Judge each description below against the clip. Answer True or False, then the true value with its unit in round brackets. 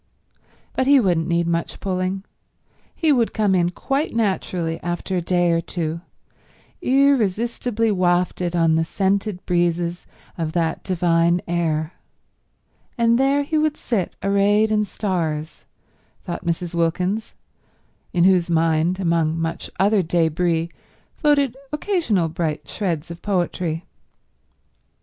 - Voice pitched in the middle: True (180 Hz)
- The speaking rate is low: True (120 wpm)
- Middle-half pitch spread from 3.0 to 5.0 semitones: True (4.0 semitones)